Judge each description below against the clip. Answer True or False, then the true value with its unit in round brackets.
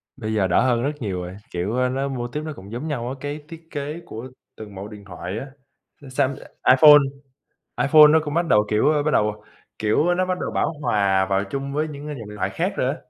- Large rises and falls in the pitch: True (6.1 semitones)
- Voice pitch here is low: True (130 Hz)